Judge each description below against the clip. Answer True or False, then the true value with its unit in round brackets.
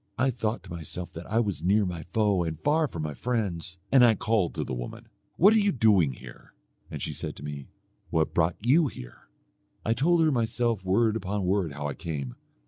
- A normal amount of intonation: False (6.3 semitones)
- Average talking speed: False (215 wpm)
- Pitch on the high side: False (100 Hz)